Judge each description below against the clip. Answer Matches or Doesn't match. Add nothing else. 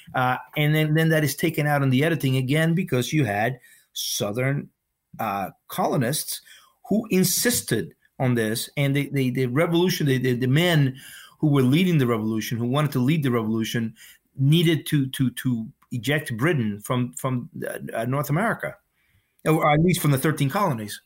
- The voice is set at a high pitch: Doesn't match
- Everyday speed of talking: Matches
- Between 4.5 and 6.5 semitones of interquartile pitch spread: Doesn't match